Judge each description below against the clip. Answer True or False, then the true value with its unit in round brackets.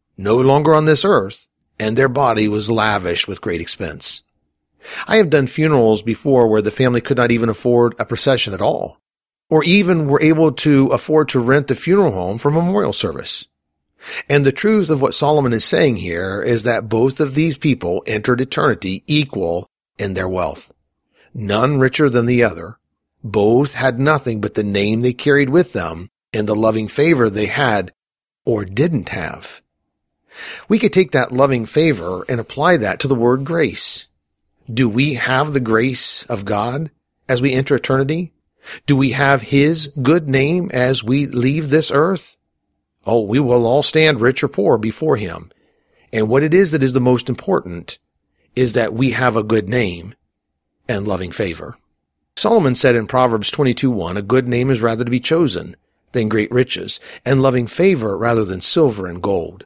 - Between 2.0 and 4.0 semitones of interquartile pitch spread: False (5.2 semitones)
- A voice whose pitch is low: True (125 Hz)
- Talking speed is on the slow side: False (175 wpm)